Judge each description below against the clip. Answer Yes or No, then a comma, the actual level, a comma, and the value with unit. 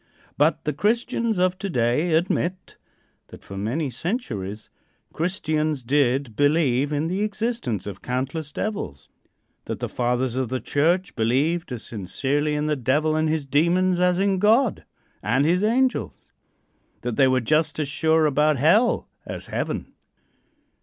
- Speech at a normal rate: Yes, average, 145 wpm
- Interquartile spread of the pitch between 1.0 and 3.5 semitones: No, wide, 5.6 semitones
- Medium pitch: Yes, medium, 150 Hz